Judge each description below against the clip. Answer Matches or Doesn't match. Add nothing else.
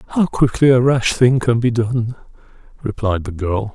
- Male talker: Matches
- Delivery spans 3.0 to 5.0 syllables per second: Matches